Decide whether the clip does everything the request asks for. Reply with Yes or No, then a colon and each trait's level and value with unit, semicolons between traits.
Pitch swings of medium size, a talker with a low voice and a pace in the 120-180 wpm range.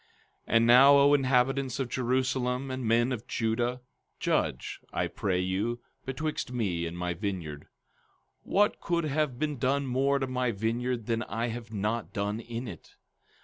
Yes: average, 3.0 semitones; low, 120 Hz; average, 165 wpm